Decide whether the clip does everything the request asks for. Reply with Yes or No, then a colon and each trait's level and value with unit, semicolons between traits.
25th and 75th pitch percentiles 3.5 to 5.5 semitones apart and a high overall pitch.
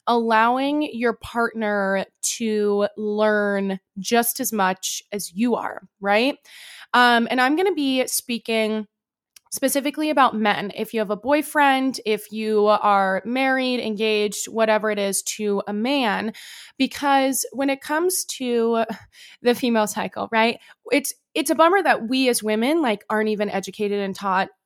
Yes: average, 3.8 semitones; high, 225 Hz